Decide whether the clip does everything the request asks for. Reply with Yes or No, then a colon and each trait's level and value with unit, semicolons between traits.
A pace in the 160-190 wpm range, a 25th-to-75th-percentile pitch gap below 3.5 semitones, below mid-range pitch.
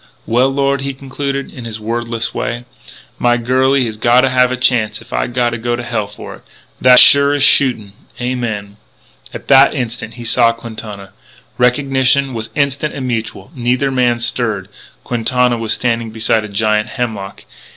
Yes: average, 165 wpm; narrow, 2.6 semitones; low, 120 Hz